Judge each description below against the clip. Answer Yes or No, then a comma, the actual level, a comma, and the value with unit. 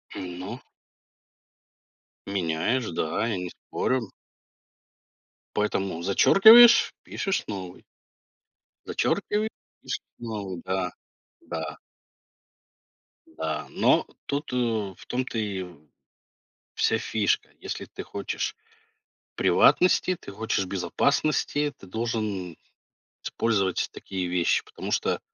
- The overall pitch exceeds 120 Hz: No, low, 100 Hz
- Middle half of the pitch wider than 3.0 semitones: Yes, average, 5.0 semitones